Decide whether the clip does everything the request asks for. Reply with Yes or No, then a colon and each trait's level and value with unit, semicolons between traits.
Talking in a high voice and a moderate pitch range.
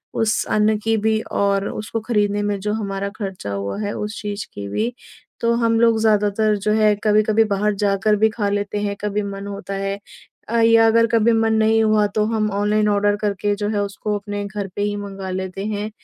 No: high, 210 Hz; narrow, 1.4 semitones